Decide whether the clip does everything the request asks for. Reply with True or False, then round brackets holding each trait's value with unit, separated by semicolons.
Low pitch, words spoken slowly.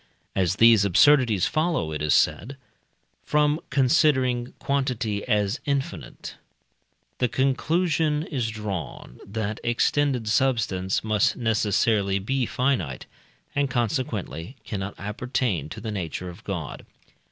True (115 Hz; 110 wpm)